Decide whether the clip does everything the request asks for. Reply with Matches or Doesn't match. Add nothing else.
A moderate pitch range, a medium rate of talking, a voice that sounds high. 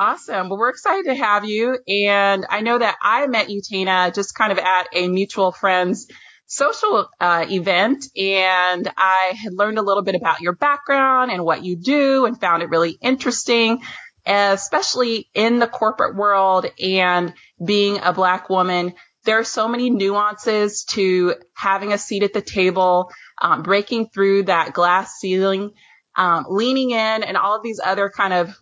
Matches